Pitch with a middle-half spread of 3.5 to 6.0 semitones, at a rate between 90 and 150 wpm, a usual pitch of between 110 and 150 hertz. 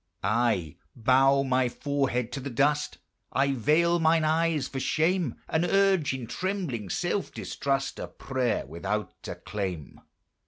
Yes: average, 5.1 semitones; average, 140 wpm; low, 135 Hz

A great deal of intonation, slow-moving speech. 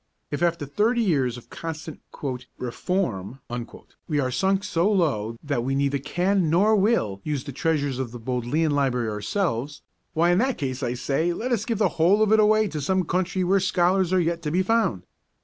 No: wide, 6.1 semitones; average, 195 wpm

